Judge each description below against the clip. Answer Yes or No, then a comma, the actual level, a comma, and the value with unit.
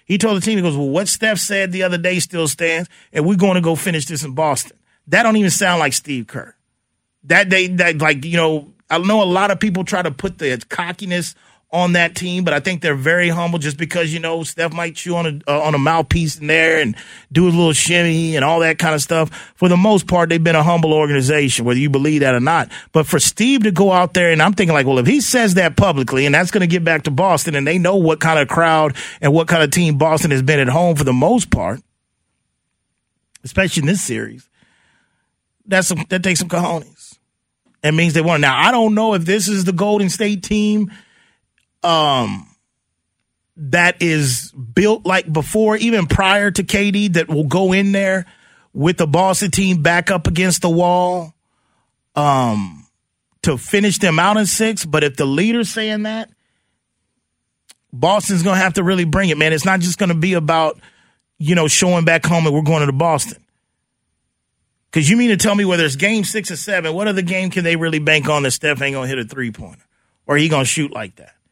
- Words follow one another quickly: Yes, fast, 220 wpm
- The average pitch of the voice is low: No, medium, 170 Hz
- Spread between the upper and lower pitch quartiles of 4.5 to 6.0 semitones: No, average, 3.7 semitones